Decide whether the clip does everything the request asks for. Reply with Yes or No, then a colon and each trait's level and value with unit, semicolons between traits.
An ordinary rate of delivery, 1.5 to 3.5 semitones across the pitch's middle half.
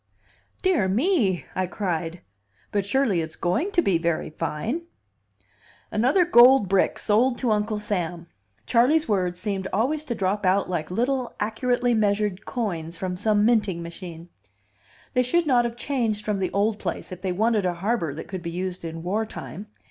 No: average, 170 wpm; average, 4.8 semitones